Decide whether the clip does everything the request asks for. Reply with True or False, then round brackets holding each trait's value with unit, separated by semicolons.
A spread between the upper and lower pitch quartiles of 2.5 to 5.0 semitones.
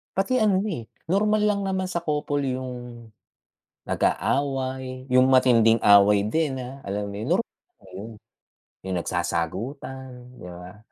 False (5.5 semitones)